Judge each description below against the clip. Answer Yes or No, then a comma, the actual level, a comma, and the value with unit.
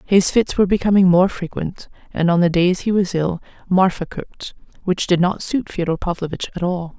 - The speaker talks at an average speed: Yes, average, 195 wpm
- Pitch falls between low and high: Yes, medium, 180 Hz